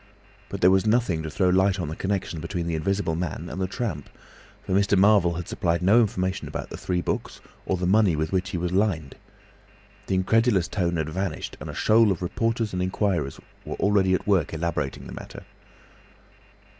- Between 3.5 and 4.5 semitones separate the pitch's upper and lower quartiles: No, average, 2.9 semitones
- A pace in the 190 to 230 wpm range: Yes, average, 195 wpm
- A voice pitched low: Yes, very low, 95 Hz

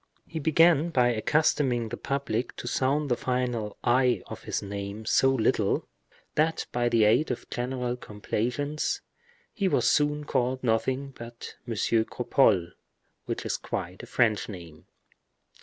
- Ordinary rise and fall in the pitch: Yes, average, 3.8 semitones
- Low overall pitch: Yes, low, 125 Hz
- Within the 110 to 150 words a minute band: Yes, average, 140 wpm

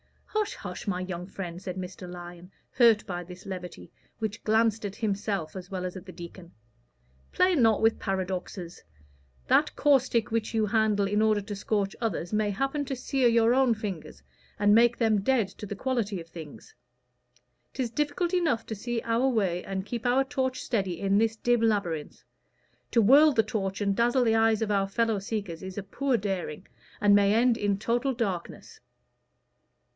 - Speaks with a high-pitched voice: Yes, high, 210 Hz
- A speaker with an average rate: Yes, average, 180 wpm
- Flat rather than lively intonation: No, average, 3.7 semitones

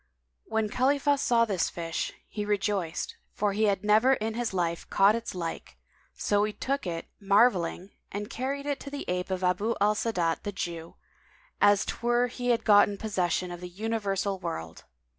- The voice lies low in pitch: No, high, 205 Hz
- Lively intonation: No, average, 4.1 semitones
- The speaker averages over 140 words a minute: Yes, average, 175 wpm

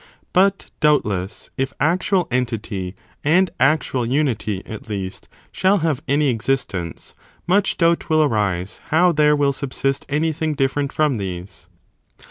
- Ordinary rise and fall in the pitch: No, wide, 6.6 semitones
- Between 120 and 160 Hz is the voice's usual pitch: Yes, low, 135 Hz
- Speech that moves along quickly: No, average, 150 wpm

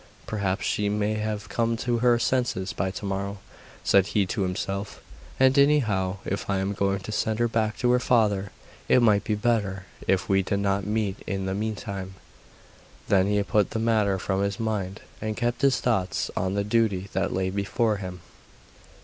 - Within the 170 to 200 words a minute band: Yes, average, 185 wpm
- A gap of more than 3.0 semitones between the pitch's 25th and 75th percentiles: No, narrow, 2.4 semitones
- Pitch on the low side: Yes, low, 100 Hz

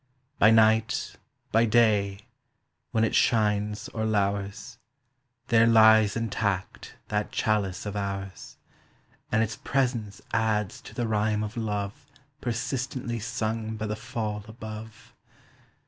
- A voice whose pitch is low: Yes, low, 110 Hz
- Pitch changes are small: Yes, narrow, 1.5 semitones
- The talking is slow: Yes, slow, 115 wpm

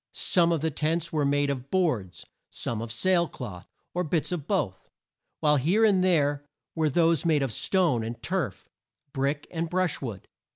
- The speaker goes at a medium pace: Yes, average, 175 wpm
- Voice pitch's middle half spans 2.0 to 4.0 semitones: No, average, 4.4 semitones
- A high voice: No, medium, 150 Hz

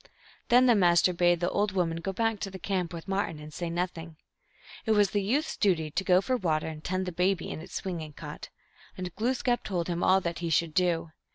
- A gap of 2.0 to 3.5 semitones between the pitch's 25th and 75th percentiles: Yes, average, 2.8 semitones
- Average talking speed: No, fast, 235 wpm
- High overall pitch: No, medium, 180 Hz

